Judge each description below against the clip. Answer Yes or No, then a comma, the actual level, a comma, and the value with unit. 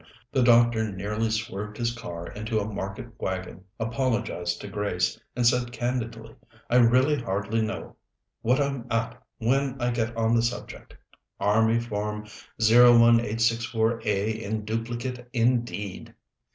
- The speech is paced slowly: Yes, slow, 130 wpm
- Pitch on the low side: Yes, low, 115 Hz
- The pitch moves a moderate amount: No, narrow, 2.1 semitones